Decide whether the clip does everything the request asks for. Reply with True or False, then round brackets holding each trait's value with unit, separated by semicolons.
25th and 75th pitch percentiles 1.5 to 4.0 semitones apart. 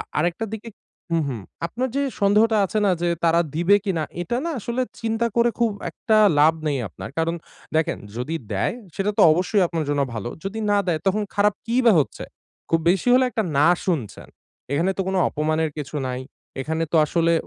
False (5.3 semitones)